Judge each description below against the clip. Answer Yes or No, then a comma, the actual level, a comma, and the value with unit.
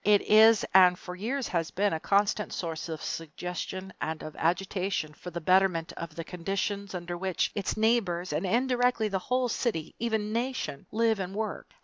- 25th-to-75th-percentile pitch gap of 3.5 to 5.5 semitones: Yes, average, 4.0 semitones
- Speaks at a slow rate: No, average, 180 wpm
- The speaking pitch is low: No, high, 190 Hz